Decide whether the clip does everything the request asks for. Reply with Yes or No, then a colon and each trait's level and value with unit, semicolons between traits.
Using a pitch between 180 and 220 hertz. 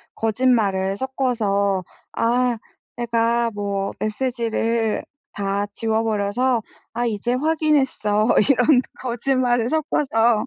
No: high, 230 Hz